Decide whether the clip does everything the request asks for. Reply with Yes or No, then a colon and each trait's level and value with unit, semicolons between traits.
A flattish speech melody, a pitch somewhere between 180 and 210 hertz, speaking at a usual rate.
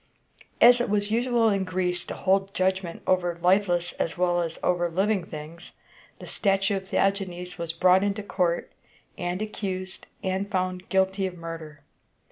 Yes: narrow, 2.0 semitones; medium, 185 Hz; average, 155 wpm